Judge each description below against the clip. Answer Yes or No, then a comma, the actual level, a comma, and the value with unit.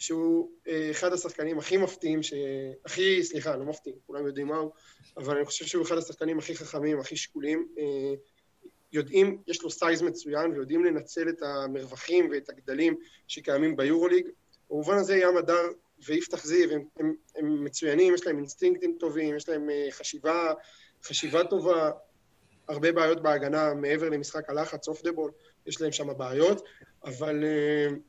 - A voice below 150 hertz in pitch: No, medium, 155 Hz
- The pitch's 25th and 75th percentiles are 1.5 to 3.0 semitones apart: Yes, average, 2.7 semitones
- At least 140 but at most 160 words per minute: Yes, fast, 150 wpm